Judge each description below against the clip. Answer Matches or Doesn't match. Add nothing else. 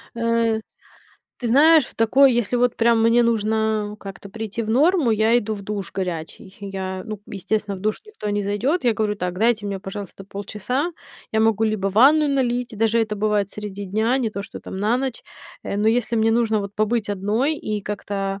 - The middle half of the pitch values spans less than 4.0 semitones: Matches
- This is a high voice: Matches